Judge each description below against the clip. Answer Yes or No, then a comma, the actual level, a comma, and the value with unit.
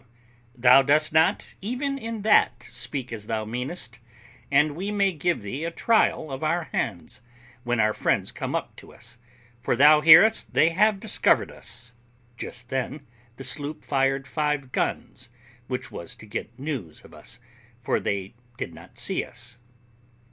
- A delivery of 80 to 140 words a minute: No, average, 160 wpm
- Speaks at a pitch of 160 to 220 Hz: No, low, 135 Hz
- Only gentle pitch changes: No, average, 5.1 semitones